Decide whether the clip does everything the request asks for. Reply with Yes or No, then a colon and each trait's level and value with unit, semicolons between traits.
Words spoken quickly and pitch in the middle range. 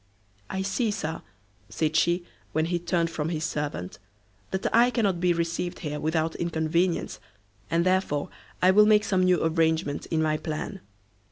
No: average, 160 wpm; medium, 170 Hz